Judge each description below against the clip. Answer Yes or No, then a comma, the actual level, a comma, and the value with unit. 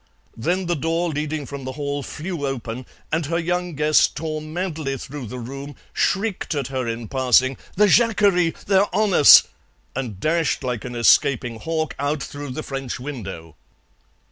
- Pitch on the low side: No, medium, 145 Hz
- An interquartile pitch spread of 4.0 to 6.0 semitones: Yes, average, 4.3 semitones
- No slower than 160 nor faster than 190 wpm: Yes, average, 165 wpm